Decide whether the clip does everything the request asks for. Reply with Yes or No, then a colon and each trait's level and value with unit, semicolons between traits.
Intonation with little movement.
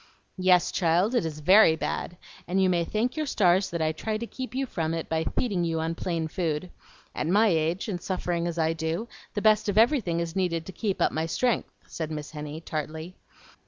No: average, 4.0 semitones